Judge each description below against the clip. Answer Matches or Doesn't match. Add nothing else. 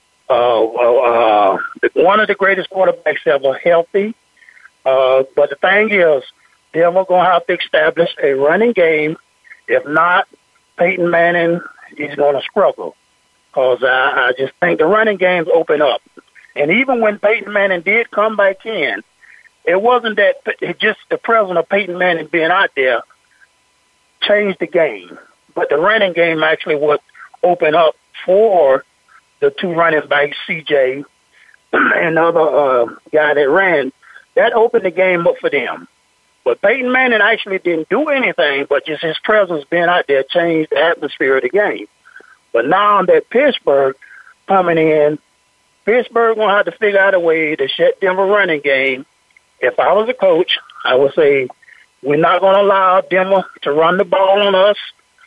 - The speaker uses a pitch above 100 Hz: Matches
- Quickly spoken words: Doesn't match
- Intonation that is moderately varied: Doesn't match